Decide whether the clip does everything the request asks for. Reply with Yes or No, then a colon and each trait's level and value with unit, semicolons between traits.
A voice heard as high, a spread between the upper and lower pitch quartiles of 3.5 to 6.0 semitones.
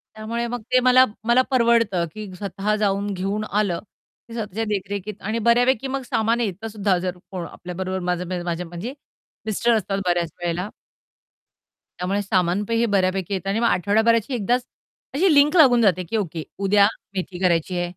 Yes: high, 205 Hz; average, 4.0 semitones